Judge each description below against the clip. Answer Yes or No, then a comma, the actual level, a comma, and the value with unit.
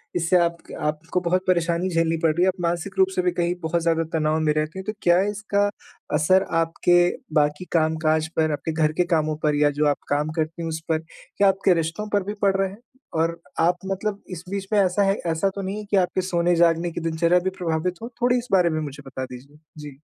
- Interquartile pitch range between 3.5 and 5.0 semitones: No, average, 3.1 semitones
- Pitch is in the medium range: Yes, medium, 170 Hz